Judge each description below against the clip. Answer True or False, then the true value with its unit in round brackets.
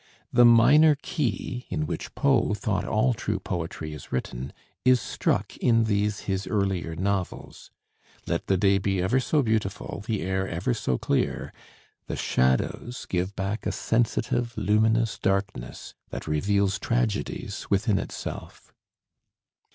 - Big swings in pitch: False (3.7 semitones)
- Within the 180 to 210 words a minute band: False (135 wpm)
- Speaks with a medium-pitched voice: False (105 Hz)